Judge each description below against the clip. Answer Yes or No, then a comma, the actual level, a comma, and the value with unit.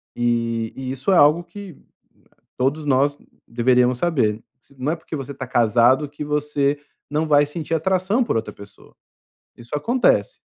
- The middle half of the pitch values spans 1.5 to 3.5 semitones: No, average, 4.3 semitones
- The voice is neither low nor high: Yes, medium, 145 Hz